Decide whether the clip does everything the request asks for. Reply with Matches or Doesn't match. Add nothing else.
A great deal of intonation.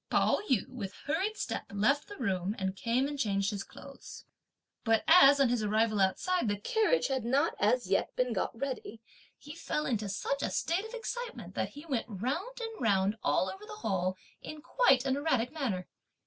Matches